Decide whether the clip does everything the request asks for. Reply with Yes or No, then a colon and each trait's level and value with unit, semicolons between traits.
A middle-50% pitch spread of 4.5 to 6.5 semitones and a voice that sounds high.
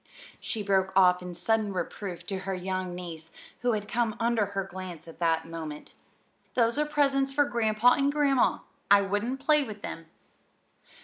Yes: average, 5.1 semitones; high, 205 Hz